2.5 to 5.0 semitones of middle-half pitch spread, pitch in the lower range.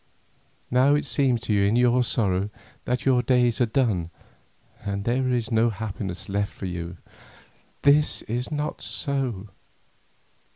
Yes: average, 4.2 semitones; low, 120 Hz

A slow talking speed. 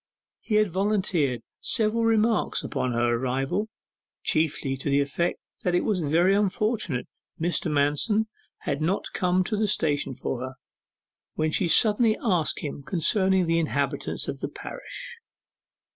No: average, 145 wpm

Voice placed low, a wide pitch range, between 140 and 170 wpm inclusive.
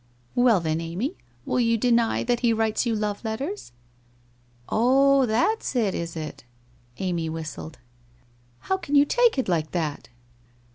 No: high, 225 Hz; wide, 7.2 semitones; average, 145 wpm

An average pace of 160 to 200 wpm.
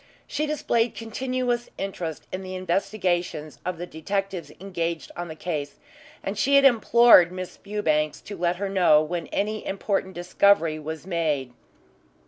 No: average, 145 wpm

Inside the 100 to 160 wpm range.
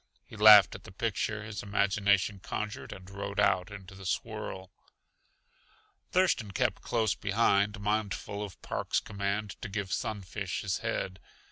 Yes: average, 140 wpm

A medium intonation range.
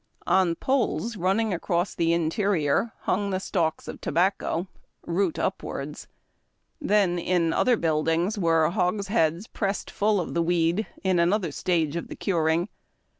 Yes: average, 3.3 semitones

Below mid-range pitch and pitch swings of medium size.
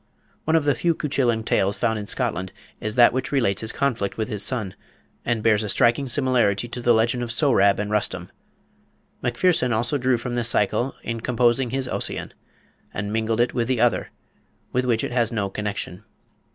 Yes: low, 120 Hz; average, 3.0 semitones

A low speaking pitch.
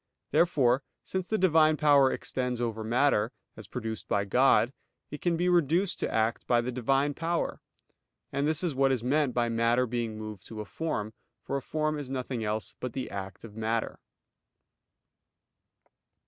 Yes: low, 125 Hz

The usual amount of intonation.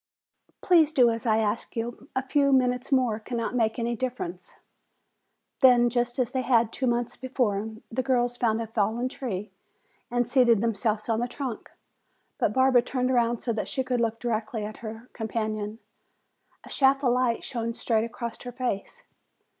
No: narrow, 2.2 semitones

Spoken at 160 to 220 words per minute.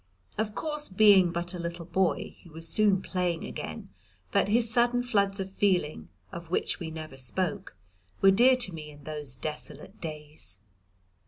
Yes: average, 165 wpm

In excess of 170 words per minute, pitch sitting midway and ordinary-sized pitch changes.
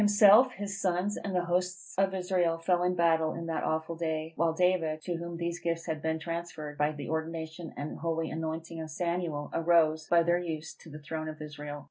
No: fast, 205 wpm; medium, 165 Hz; narrow, 1.9 semitones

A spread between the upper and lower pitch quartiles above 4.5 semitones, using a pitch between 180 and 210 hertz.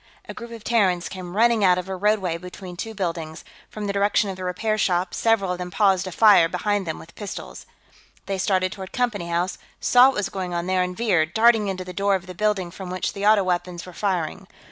No: narrow, 2.5 semitones; high, 190 Hz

